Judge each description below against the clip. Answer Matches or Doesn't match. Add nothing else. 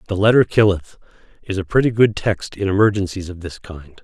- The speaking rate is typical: Matches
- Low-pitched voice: Matches